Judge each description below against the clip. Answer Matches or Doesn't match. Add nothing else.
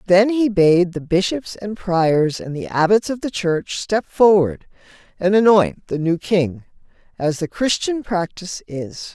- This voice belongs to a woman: Matches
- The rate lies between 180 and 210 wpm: Doesn't match